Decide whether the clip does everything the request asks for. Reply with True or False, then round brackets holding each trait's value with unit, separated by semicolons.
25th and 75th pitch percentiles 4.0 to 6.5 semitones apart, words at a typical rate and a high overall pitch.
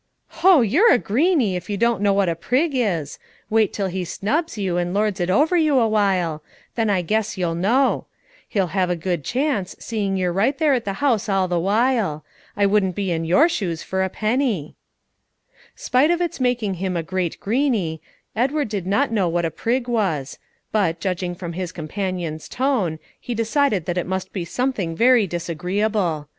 True (5.4 semitones; 190 wpm; 200 Hz)